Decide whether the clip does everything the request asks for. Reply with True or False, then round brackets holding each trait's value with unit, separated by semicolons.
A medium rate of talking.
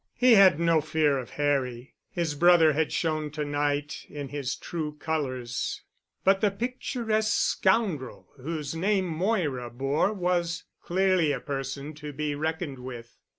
True (145 wpm)